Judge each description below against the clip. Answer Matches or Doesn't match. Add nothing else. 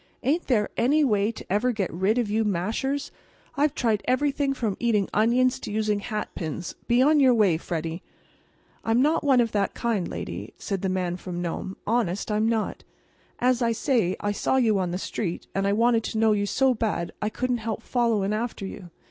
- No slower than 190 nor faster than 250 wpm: Matches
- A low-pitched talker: Doesn't match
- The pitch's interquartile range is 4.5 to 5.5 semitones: Doesn't match